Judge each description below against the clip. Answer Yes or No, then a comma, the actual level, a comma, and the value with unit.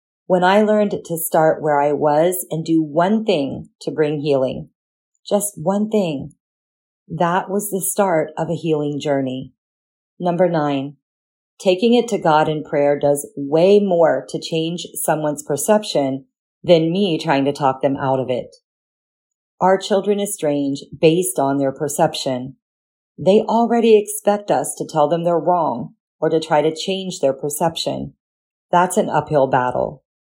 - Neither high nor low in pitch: Yes, medium, 160 Hz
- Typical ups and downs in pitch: Yes, average, 4.8 semitones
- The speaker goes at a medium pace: Yes, average, 150 wpm